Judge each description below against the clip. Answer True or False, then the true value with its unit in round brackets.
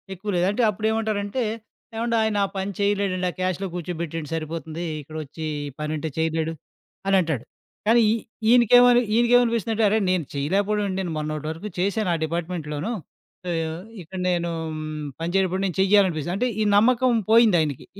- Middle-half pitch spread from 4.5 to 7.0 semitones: True (5.0 semitones)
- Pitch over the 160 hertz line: True (185 Hz)